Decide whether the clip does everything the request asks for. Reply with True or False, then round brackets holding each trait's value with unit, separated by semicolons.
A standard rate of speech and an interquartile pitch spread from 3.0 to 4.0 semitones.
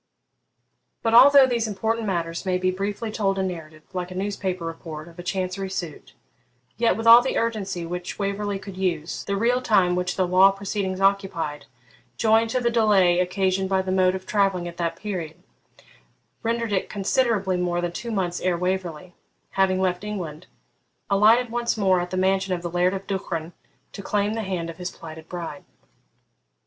False (180 wpm; 2.6 semitones)